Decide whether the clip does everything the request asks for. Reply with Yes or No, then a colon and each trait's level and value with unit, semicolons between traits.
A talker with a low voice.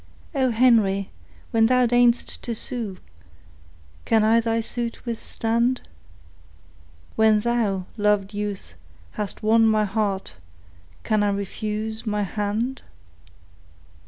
No: high, 220 Hz